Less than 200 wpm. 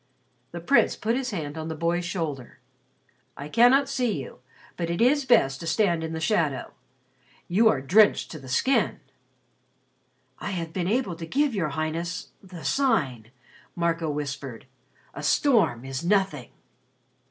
Yes: average, 155 wpm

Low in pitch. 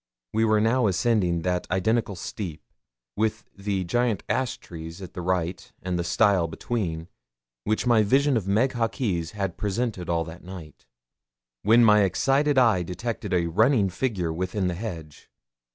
Yes: low, 100 Hz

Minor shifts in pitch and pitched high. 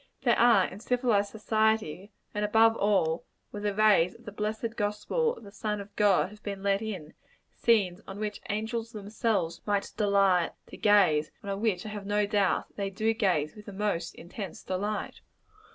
Yes: narrow, 1.8 semitones; high, 205 Hz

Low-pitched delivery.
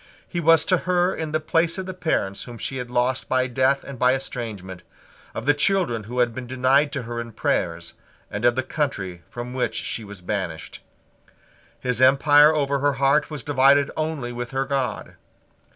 Yes: low, 130 Hz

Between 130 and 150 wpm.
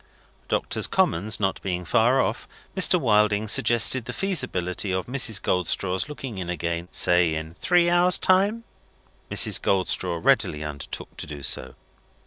Yes: average, 140 wpm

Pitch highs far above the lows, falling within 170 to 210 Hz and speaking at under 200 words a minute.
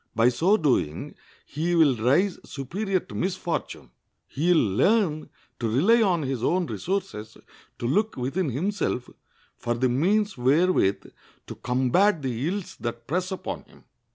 No: wide, 7.3 semitones; medium, 155 Hz; average, 145 wpm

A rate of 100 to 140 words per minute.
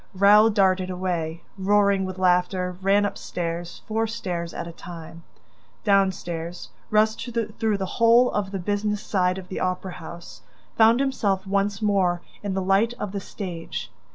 No: average, 160 wpm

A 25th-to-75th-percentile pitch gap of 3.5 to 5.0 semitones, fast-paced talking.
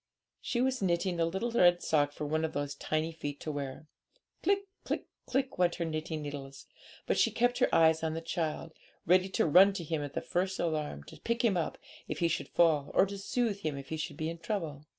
Yes: average, 4.0 semitones; fast, 230 wpm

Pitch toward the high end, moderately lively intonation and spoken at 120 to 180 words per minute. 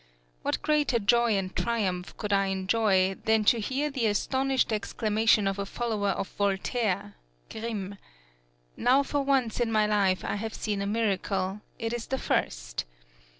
Yes: high, 215 Hz; average, 3.2 semitones; average, 155 wpm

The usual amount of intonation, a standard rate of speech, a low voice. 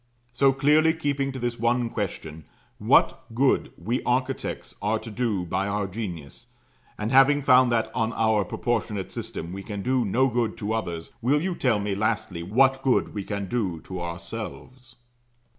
Yes: average, 4.4 semitones; average, 170 wpm; low, 115 Hz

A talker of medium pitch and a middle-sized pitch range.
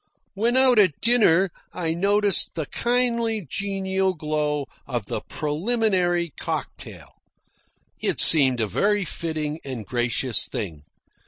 No: medium, 175 Hz; wide, 5.8 semitones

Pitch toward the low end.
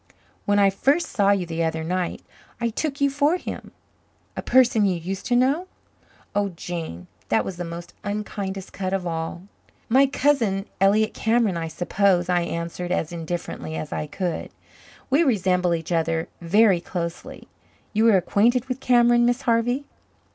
No: high, 195 Hz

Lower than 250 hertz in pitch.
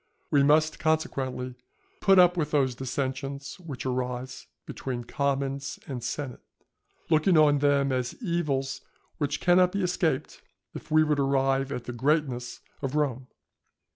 Yes: medium, 140 Hz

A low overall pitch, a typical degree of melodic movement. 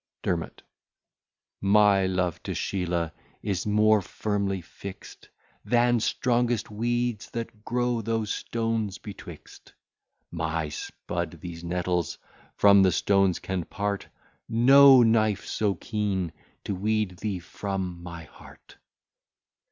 Yes: low, 100 Hz; average, 3.8 semitones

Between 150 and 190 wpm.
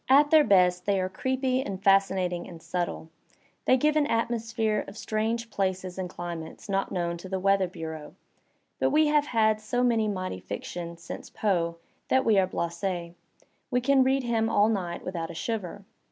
Yes: average, 180 wpm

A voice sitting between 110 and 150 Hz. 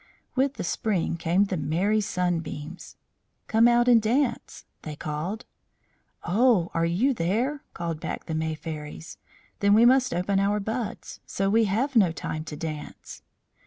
No: high, 195 Hz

